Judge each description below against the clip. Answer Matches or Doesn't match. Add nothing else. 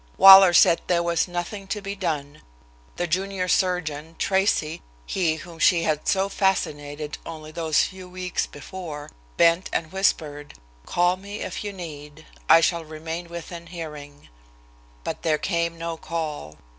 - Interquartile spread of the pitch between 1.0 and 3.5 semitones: Matches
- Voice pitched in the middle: Matches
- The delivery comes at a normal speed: Matches